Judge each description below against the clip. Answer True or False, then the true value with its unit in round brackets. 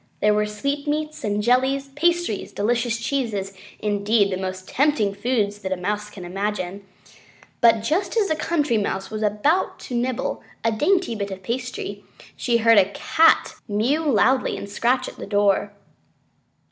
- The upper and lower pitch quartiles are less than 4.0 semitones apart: False (5.2 semitones)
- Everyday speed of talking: True (160 wpm)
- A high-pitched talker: True (225 Hz)